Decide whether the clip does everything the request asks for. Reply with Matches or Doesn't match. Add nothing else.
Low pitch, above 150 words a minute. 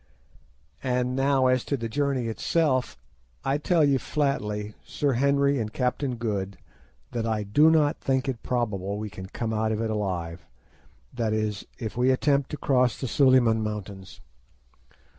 Matches